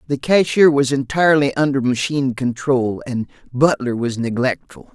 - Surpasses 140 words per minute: No, slow, 135 wpm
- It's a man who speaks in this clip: Yes, male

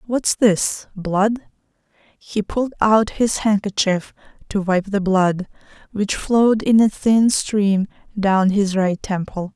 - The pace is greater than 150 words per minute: No, average, 140 wpm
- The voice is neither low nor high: No, high, 205 Hz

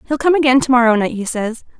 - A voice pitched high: Yes, very high, 250 Hz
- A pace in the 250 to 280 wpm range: Yes, fast, 270 wpm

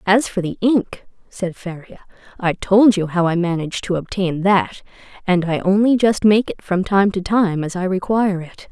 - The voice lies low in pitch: No, high, 190 Hz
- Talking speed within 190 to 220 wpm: Yes, average, 195 wpm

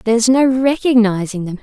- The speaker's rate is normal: Yes, average, 150 wpm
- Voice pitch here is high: Yes, high, 235 Hz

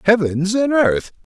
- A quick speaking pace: No, slow, 135 wpm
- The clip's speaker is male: Yes, male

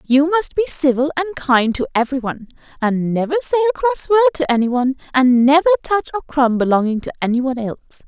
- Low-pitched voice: No, very high, 265 Hz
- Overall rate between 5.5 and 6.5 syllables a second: Yes, 5.8 syllables/s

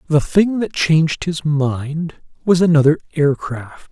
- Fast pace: No, average, 140 wpm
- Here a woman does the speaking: No, male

